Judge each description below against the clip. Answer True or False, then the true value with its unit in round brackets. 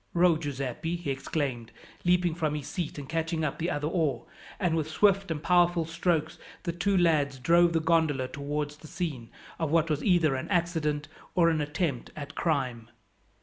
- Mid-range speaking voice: True (160 Hz)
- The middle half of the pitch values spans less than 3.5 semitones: True (2.9 semitones)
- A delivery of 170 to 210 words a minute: True (180 wpm)